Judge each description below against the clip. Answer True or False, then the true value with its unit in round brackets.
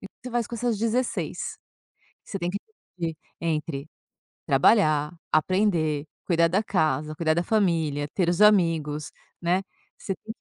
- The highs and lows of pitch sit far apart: False (4.8 semitones)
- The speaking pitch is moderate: True (170 Hz)